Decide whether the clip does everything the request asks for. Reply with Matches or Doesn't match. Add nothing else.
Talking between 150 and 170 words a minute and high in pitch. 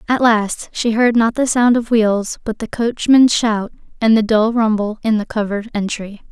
Doesn't match